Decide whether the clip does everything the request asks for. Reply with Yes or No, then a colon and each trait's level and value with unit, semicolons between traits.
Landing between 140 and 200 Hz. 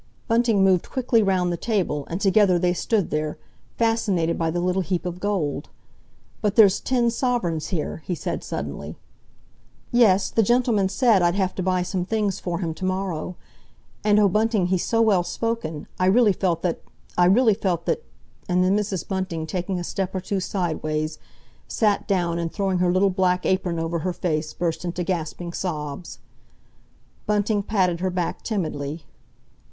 Yes: medium, 185 Hz